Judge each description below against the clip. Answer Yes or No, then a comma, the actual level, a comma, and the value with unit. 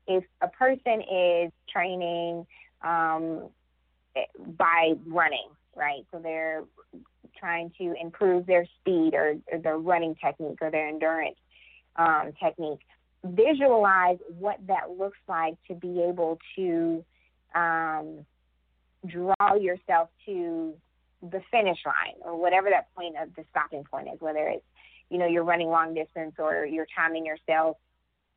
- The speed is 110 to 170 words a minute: Yes, slow, 135 wpm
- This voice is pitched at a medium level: Yes, medium, 165 Hz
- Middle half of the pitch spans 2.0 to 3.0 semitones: Yes, narrow, 2.5 semitones